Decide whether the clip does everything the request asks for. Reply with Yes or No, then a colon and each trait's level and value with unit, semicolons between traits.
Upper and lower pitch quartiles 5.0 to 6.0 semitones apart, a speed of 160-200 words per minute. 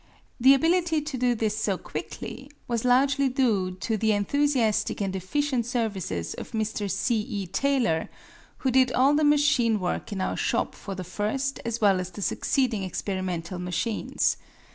Yes: wide, 5.4 semitones; average, 165 wpm